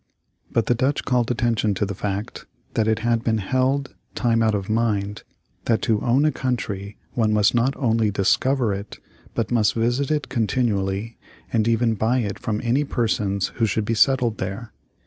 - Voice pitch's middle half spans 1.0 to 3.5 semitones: Yes, average, 2.7 semitones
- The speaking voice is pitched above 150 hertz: No, low, 115 Hz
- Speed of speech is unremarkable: Yes, average, 180 wpm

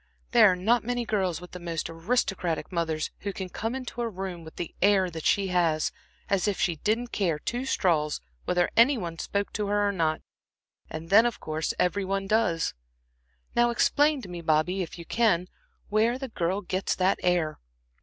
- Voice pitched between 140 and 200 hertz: Yes, high, 190 Hz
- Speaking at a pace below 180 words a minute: No, average, 195 wpm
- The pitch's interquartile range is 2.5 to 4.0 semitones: No, average, 4.4 semitones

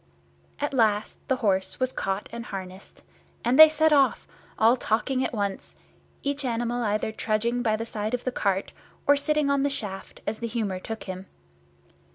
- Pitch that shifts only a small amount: No, average, 4.0 semitones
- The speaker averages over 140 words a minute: Yes, average, 180 wpm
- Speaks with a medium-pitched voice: No, high, 230 Hz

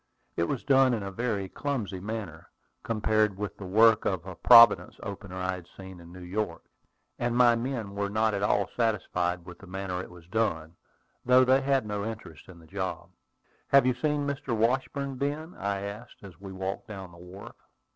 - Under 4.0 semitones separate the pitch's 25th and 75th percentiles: No, average, 4.3 semitones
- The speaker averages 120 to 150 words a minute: No, average, 195 wpm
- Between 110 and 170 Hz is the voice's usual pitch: No, low, 100 Hz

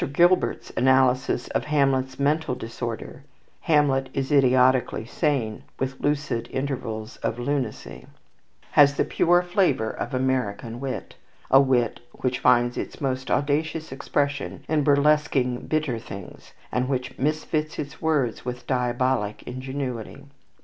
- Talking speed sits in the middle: No, slow, 120 wpm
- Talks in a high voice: No, low, 130 Hz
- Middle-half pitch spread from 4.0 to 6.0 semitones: No, average, 2.7 semitones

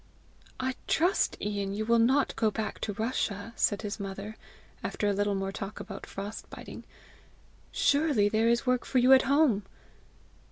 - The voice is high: Yes, high, 215 Hz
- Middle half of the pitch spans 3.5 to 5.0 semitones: Yes, average, 3.8 semitones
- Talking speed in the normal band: Yes, average, 165 wpm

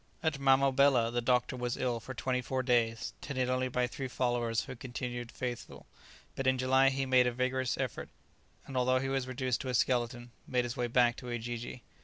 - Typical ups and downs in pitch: No, narrow, 1.4 semitones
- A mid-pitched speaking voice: No, low, 125 Hz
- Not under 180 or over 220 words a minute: Yes, average, 200 wpm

